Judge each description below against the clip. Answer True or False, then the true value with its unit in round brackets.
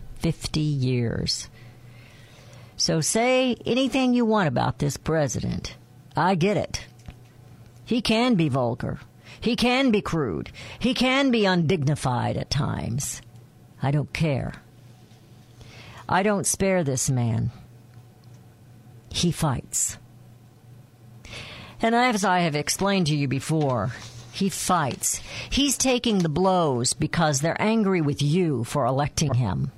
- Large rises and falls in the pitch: True (7.2 semitones)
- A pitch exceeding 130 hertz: True (140 Hz)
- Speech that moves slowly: True (120 wpm)